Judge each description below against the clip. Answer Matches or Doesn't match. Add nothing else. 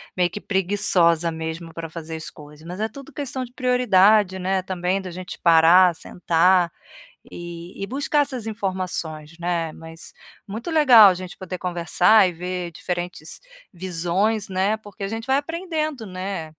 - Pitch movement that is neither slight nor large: Matches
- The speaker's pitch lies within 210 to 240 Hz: Doesn't match